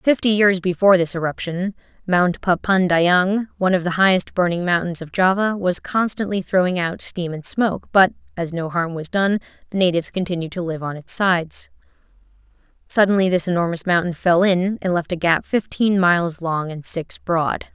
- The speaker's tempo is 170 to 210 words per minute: Yes, average, 175 wpm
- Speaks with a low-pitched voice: No, medium, 180 Hz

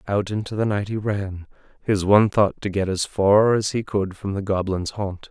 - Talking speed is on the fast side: Yes, fast, 225 wpm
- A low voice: Yes, low, 100 Hz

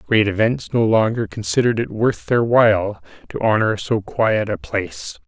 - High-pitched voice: No, low, 110 Hz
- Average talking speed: Yes, average, 170 wpm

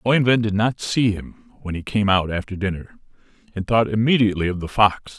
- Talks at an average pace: Yes, average, 195 wpm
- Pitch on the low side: Yes, low, 105 Hz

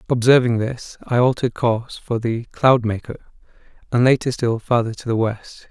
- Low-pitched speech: Yes, low, 120 Hz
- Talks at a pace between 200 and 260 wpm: No, average, 160 wpm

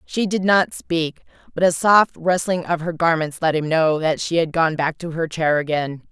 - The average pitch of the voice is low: No, medium, 165 Hz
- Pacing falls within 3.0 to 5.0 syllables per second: Yes, 4.6 syllables/s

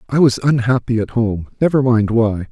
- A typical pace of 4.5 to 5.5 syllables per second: Yes, 5.1 syllables/s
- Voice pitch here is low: Yes, low, 120 Hz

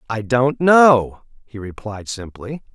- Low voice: Yes, low, 120 Hz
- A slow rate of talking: Yes, slow, 130 wpm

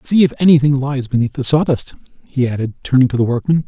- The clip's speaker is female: No, male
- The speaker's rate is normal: No, fast, 210 wpm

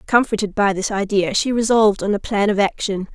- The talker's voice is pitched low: No, high, 205 Hz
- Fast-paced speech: Yes, fast, 210 wpm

